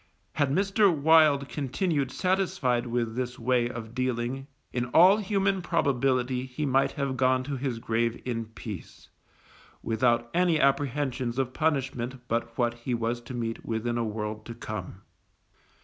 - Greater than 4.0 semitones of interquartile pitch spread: No, average, 3.2 semitones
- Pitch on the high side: No, low, 125 Hz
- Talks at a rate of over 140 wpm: Yes, average, 150 wpm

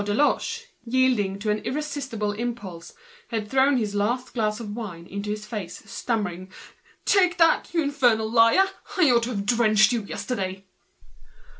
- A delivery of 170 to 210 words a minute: No, average, 160 wpm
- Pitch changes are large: No, average, 3.9 semitones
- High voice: Yes, high, 225 Hz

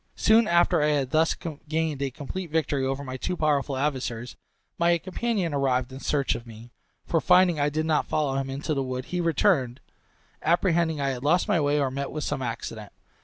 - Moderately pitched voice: Yes, medium, 145 Hz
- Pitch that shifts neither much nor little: Yes, average, 3.8 semitones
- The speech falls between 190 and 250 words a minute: Yes, average, 200 wpm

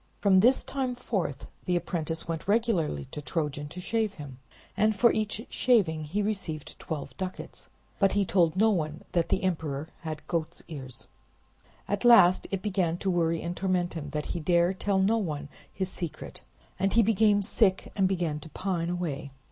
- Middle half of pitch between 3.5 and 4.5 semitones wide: Yes, average, 4.1 semitones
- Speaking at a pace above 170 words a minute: Yes, average, 180 wpm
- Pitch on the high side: No, medium, 180 Hz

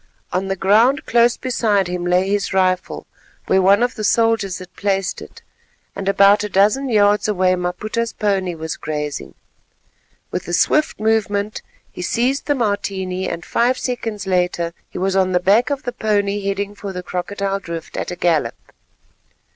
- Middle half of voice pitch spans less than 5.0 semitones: Yes, average, 2.8 semitones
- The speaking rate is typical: Yes, average, 170 wpm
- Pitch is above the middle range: Yes, high, 200 Hz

